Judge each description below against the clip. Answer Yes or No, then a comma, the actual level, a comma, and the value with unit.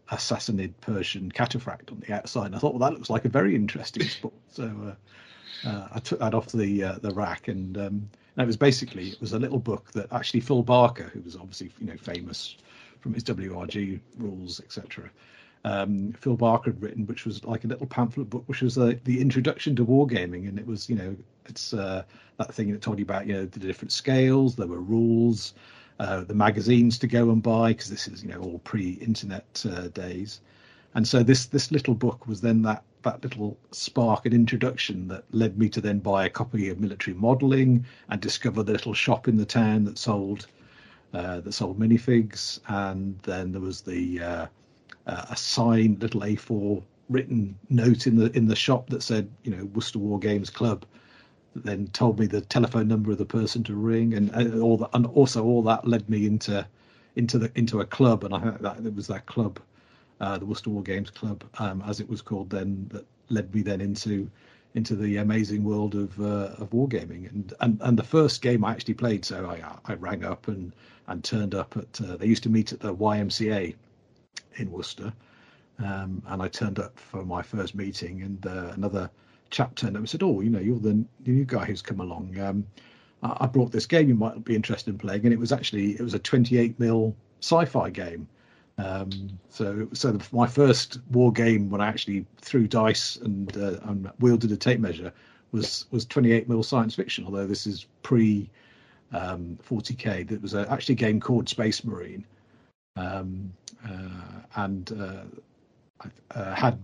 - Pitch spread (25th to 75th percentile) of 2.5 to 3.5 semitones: Yes, average, 2.9 semitones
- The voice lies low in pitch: Yes, low, 110 Hz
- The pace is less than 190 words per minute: No, fast, 205 wpm